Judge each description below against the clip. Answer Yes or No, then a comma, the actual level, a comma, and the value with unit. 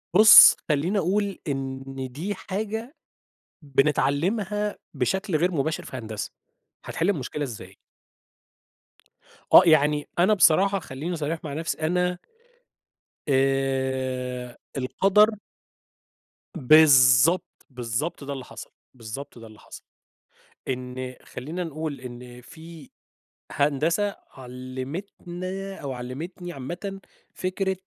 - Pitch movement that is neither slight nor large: No, wide, 5.8 semitones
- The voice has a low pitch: No, medium, 150 Hz